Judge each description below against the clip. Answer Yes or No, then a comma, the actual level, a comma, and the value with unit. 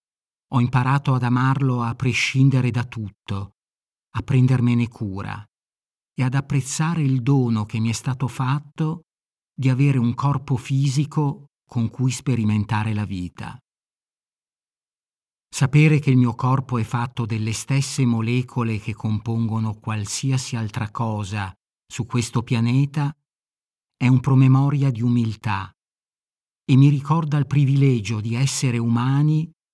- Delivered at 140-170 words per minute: No, average, 125 wpm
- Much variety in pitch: No, average, 3.3 semitones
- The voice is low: Yes, low, 125 Hz